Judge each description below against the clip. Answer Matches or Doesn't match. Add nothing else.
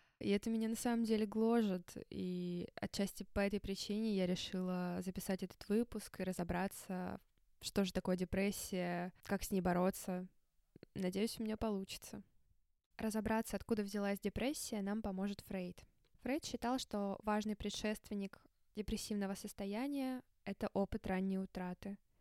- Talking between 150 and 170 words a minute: Doesn't match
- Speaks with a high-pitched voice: Matches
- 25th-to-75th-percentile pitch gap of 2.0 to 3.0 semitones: Matches